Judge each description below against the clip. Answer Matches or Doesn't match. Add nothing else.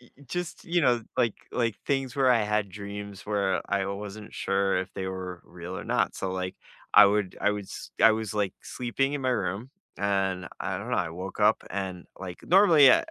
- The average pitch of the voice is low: Matches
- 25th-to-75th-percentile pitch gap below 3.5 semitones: Doesn't match